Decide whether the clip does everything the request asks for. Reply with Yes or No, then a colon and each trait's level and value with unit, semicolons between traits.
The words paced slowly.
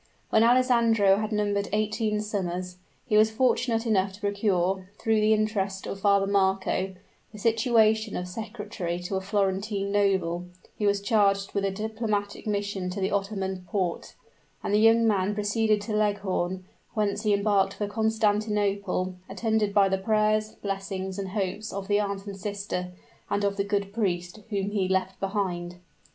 No: average, 160 wpm